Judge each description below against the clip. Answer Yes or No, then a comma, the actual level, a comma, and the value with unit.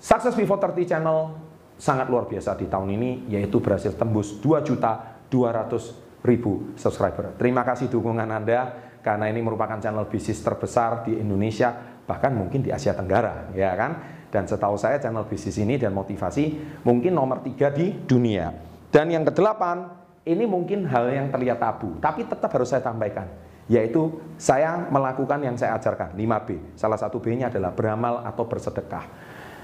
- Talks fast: Yes, fast, 150 wpm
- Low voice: Yes, low, 120 Hz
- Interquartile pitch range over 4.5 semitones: Yes, average, 5.1 semitones